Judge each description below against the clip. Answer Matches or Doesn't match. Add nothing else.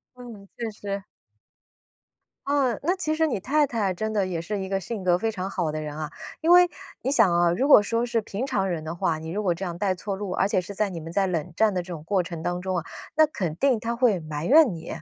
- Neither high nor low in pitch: Doesn't match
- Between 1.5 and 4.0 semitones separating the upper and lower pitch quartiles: Doesn't match